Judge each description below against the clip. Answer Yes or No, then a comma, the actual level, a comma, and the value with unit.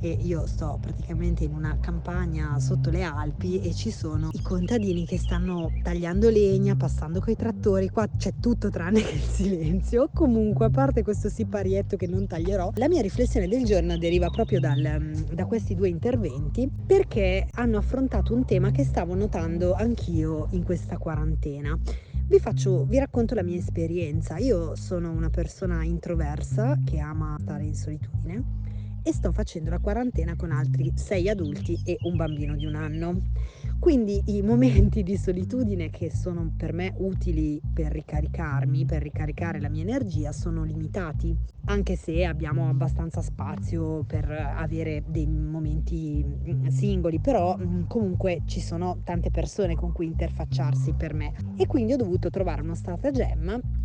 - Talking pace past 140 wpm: Yes, average, 155 wpm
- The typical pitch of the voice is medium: No, low, 100 Hz